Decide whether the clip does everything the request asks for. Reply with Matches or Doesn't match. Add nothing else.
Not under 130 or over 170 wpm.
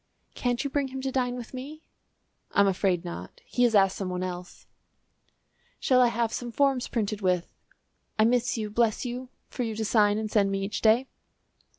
Doesn't match